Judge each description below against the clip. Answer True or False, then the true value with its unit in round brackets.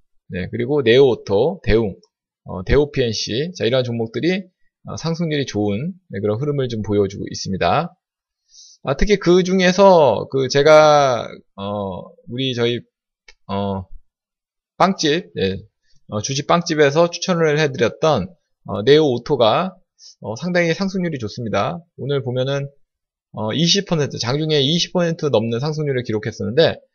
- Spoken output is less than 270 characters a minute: True (260 characters per minute)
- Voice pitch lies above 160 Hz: False (140 Hz)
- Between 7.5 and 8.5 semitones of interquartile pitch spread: True (7.8 semitones)